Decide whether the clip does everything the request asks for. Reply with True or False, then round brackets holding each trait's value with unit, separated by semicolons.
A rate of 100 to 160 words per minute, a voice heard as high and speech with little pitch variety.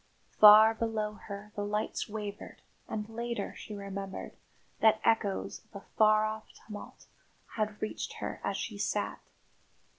True (140 wpm; 215 Hz; 1.1 semitones)